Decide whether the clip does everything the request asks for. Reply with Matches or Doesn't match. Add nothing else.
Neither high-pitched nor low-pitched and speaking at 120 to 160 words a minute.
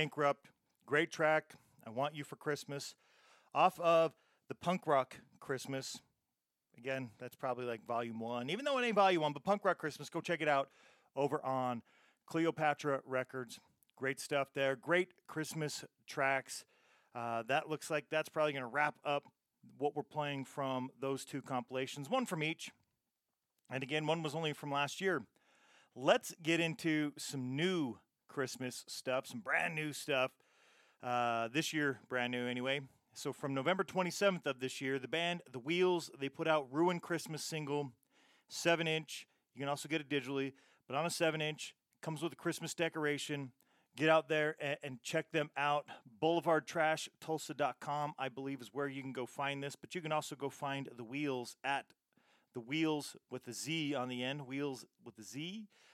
Doesn't match